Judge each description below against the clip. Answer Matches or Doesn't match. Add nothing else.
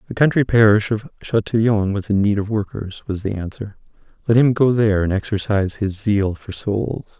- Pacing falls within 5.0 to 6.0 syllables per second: Matches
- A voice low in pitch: Matches